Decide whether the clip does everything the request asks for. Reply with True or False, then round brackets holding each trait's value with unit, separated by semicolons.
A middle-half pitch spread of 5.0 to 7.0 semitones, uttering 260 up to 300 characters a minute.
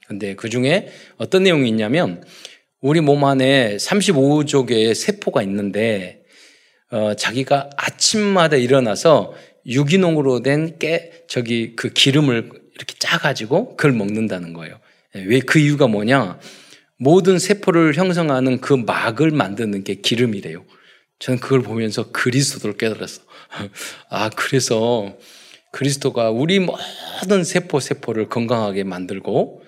True (5.5 semitones; 275 characters per minute)